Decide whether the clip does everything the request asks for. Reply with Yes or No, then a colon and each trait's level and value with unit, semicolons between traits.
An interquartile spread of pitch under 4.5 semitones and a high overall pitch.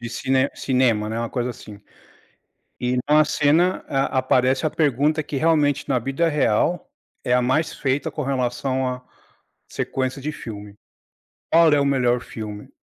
No: average, 3.2 semitones; low, 130 Hz